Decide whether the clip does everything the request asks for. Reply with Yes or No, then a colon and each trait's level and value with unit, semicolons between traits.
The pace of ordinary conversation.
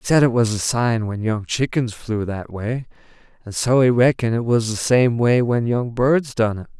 No: fast, 230 wpm